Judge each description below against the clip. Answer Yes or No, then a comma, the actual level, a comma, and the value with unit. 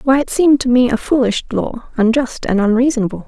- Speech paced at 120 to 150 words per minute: No, average, 200 wpm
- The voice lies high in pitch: Yes, very high, 250 Hz